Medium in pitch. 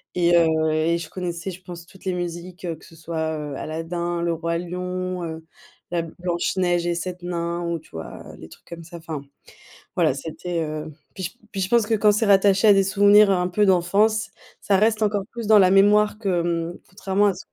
Yes: medium, 175 Hz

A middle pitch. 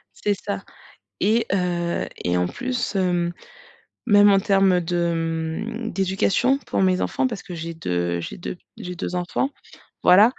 Yes: medium, 180 Hz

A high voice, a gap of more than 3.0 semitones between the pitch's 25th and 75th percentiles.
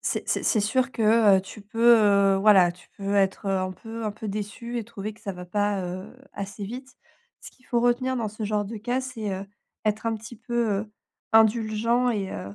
No: high, 215 Hz; average, 2.7 semitones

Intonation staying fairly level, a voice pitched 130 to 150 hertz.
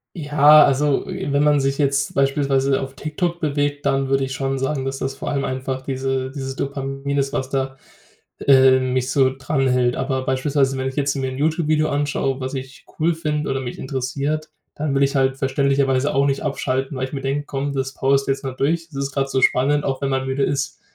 Yes: narrow, 1.3 semitones; low, 135 Hz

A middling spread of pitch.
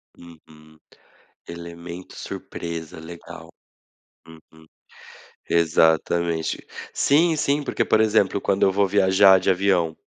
Yes: average, 3.3 semitones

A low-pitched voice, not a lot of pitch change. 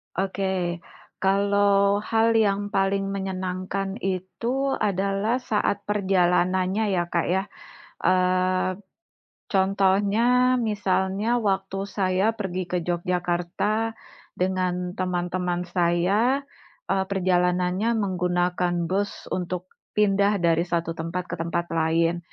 No: high, 190 Hz; narrow, 2.1 semitones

